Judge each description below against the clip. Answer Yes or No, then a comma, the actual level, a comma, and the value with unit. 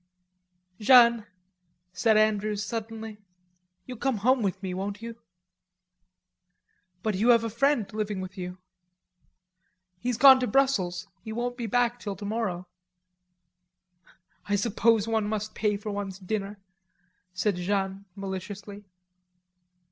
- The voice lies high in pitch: Yes, high, 215 Hz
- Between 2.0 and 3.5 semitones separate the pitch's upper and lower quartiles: Yes, average, 2.8 semitones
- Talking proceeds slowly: Yes, slow, 120 wpm